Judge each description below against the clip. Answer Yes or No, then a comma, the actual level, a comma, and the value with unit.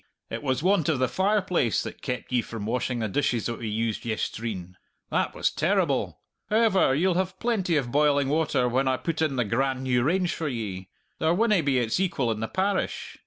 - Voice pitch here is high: No, low, 135 Hz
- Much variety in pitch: Yes, wide, 6.9 semitones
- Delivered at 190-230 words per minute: Yes, fast, 205 wpm